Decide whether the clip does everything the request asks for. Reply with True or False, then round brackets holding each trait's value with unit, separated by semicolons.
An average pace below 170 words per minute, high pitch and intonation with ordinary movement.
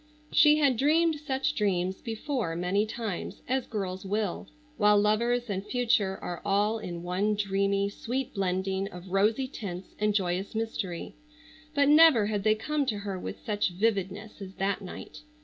True (160 wpm; 210 Hz; 3.6 semitones)